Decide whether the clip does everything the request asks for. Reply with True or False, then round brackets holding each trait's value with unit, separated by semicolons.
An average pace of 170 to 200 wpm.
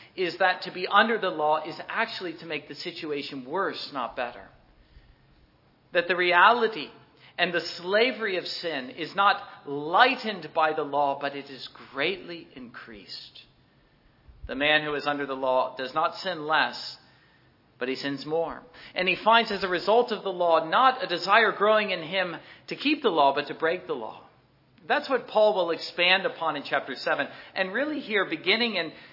True (180 wpm)